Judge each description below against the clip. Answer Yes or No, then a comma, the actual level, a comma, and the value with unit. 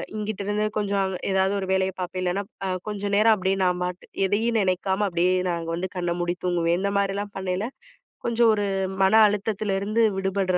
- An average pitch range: No, narrow, 2.1 semitones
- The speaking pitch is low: No, high, 195 Hz